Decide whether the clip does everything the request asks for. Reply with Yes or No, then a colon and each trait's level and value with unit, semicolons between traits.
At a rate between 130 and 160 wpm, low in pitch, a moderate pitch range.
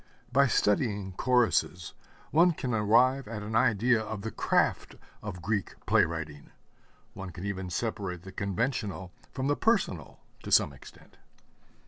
Yes: average, 140 wpm; low, 105 Hz; average, 4.6 semitones